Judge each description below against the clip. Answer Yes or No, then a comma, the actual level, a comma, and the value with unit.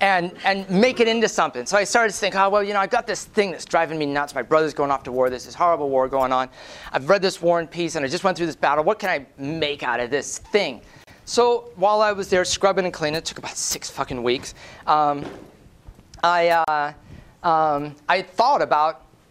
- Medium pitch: Yes, medium, 165 Hz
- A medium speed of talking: No, fast, 240 wpm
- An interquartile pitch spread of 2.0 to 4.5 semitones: No, average, 5.2 semitones